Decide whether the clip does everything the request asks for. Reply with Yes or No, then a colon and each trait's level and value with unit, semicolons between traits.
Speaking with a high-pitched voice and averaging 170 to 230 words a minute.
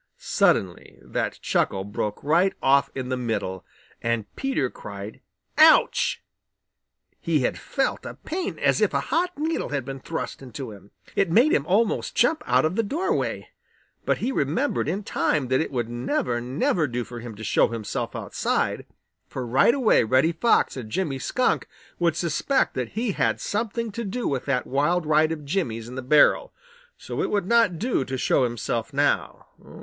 No: medium, 145 Hz; average, 180 wpm